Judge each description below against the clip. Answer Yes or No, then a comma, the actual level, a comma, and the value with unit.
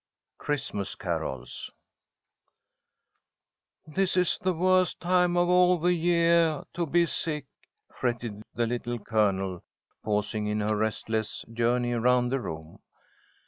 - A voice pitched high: No, low, 125 Hz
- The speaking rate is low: Yes, slow, 115 wpm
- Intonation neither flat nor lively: No, wide, 8.2 semitones